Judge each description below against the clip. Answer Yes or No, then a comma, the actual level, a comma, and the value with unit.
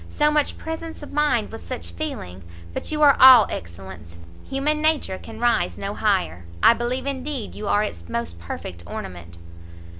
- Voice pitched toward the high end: Yes, high, 220 Hz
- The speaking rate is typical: Yes, average, 170 wpm